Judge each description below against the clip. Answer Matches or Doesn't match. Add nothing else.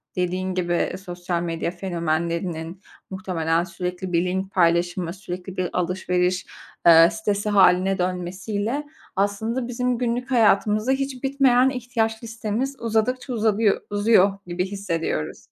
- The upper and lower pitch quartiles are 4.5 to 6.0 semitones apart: Doesn't match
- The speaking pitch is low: Doesn't match